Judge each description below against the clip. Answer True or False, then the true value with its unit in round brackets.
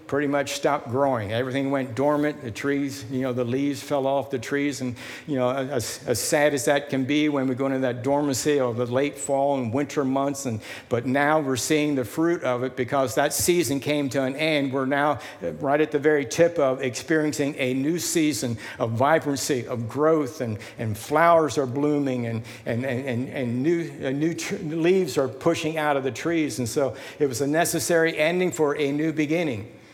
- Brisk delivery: True (210 wpm)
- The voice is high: False (140 Hz)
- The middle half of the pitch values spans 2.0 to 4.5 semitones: True (2.6 semitones)